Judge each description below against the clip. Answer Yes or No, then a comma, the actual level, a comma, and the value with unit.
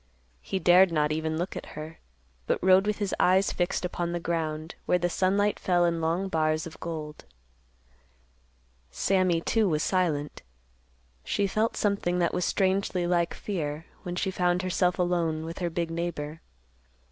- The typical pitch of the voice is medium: Yes, medium, 175 Hz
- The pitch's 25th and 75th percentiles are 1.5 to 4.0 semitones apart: Yes, narrow, 2.4 semitones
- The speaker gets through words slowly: No, average, 160 wpm